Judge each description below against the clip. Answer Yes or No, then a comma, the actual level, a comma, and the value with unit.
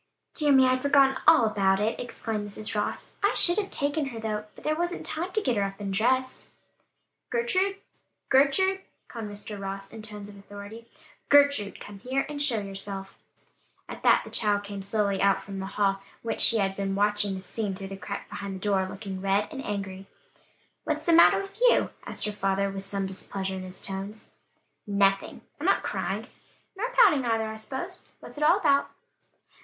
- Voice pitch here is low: No, high, 210 Hz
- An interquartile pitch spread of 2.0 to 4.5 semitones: No, wide, 5.6 semitones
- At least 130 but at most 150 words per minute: No, average, 190 wpm